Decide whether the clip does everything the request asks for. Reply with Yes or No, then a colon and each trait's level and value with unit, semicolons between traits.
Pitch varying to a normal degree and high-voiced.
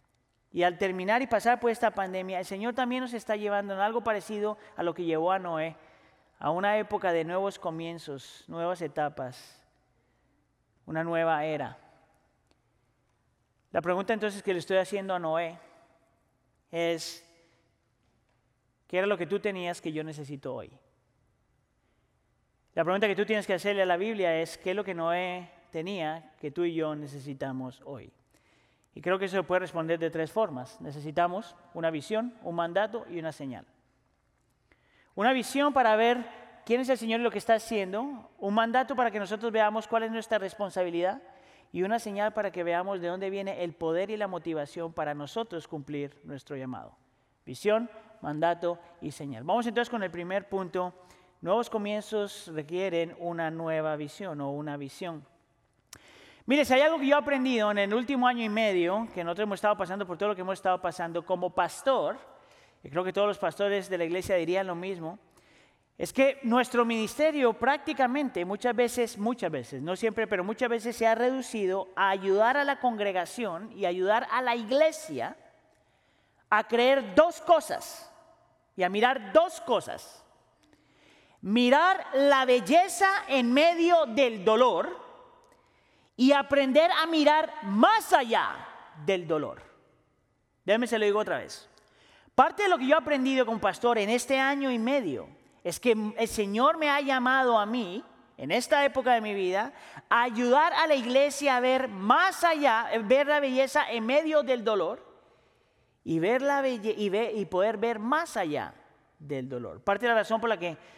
No: wide, 6.2 semitones; high, 205 Hz